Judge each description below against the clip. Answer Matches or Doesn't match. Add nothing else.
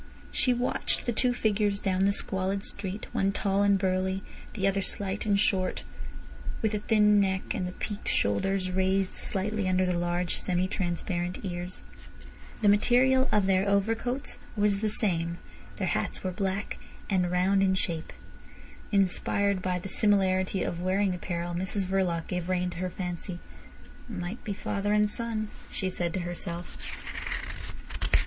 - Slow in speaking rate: Doesn't match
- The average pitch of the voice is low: Doesn't match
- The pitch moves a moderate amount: Doesn't match